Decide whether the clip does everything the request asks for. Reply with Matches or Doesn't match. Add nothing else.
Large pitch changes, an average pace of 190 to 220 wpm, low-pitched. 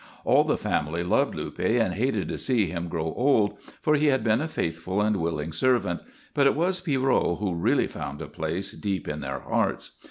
Matches